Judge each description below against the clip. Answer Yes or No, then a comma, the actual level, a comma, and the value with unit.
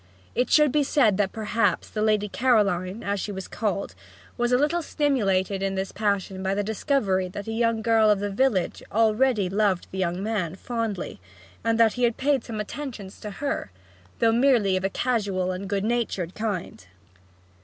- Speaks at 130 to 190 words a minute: Yes, average, 185 wpm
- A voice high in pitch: Yes, high, 210 Hz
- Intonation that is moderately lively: Yes, average, 3.4 semitones